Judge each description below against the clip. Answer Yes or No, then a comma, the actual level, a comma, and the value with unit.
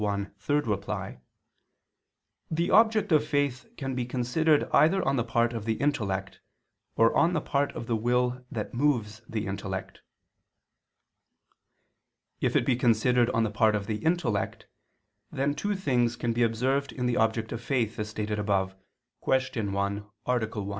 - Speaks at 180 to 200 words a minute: No, average, 160 wpm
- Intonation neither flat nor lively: Yes, average, 4.3 semitones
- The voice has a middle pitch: No, low, 120 Hz